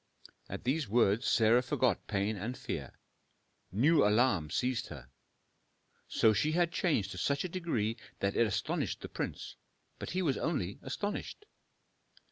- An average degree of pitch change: No, wide, 6.9 semitones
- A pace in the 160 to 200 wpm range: No, average, 145 wpm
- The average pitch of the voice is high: No, low, 120 Hz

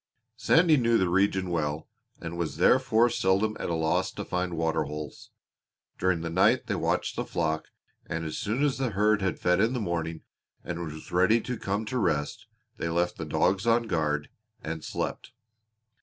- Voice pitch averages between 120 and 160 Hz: No, very low, 90 Hz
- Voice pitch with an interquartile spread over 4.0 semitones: Yes, average, 5.2 semitones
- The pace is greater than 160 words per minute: Yes, average, 185 wpm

